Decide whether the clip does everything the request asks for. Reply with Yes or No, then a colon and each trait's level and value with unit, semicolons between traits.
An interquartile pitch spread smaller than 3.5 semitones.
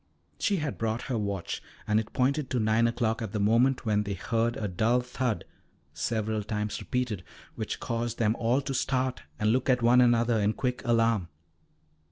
Yes: narrow, 2.6 semitones